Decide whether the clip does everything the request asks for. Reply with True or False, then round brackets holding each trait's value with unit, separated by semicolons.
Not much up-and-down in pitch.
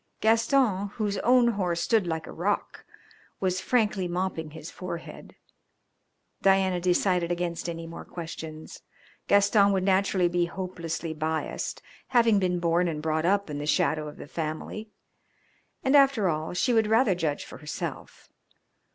False (3.6 semitones)